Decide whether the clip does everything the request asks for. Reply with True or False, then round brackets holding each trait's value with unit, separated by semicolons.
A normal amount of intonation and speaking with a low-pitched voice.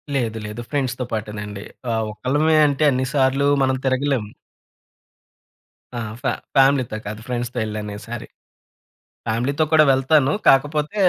True (4.1 semitones; 130 Hz)